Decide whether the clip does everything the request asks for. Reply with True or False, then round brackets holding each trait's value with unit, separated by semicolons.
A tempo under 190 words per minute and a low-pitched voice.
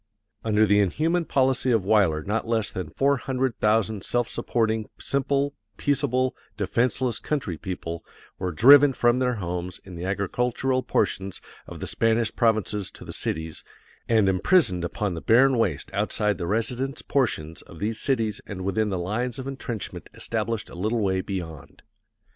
True (160 wpm; 110 Hz)